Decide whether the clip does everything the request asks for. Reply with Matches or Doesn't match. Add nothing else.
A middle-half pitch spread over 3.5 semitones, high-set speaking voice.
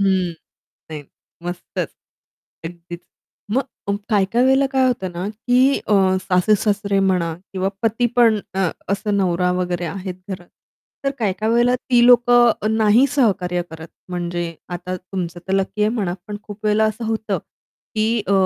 Matches